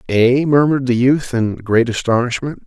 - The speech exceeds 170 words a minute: No, average, 155 wpm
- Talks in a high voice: No, low, 125 Hz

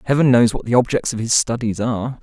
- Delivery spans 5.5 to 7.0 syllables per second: Yes, 6.4 syllables/s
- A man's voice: Yes, male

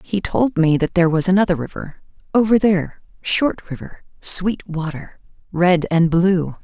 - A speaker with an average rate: Yes, average, 145 wpm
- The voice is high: No, medium, 180 Hz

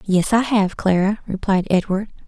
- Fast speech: No, average, 160 wpm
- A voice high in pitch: Yes, high, 200 Hz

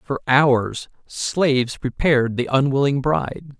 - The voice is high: No, low, 135 Hz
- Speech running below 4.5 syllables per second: Yes, 4.0 syllables/s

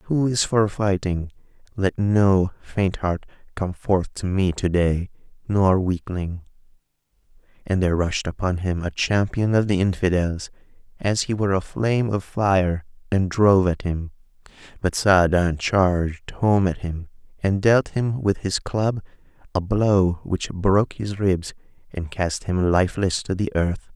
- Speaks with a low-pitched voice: Yes, very low, 95 Hz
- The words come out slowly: No, average, 155 wpm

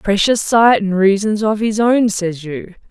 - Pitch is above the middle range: Yes, high, 205 Hz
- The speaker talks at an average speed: Yes, average, 185 wpm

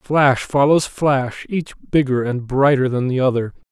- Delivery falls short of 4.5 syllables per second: Yes, 4.2 syllables/s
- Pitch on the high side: No, low, 135 Hz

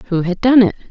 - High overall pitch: Yes, high, 210 Hz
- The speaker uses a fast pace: Yes, fast, 265 wpm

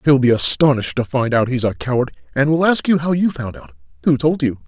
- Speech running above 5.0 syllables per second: Yes, 5.9 syllables/s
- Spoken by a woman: No, male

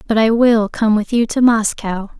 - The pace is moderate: No, fast, 220 wpm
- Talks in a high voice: Yes, high, 220 Hz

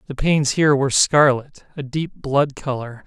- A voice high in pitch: No, medium, 140 Hz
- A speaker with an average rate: Yes, average, 155 wpm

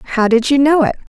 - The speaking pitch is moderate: No, very high, 260 Hz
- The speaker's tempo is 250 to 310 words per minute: Yes, fast, 260 wpm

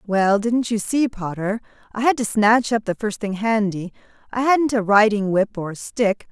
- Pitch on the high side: Yes, high, 215 Hz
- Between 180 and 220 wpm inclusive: Yes, average, 200 wpm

